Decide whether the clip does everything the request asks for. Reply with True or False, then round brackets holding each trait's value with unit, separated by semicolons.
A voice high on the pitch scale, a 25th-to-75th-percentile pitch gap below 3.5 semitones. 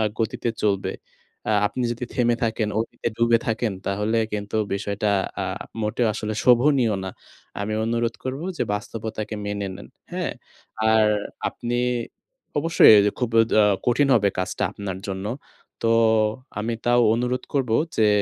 False (110 Hz; 2.6 semitones)